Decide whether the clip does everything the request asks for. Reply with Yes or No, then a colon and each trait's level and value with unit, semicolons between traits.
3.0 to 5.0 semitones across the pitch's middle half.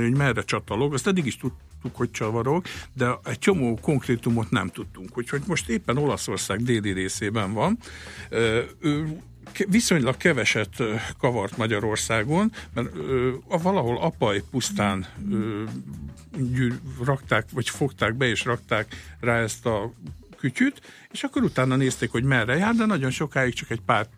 Yes: average, 4.3 semitones